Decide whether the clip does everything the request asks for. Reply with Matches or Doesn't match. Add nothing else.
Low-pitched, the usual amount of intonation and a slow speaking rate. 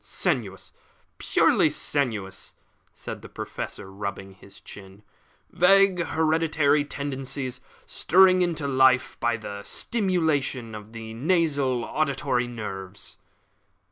Doesn't match